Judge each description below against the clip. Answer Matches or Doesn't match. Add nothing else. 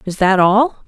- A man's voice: Doesn't match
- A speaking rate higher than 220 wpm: Doesn't match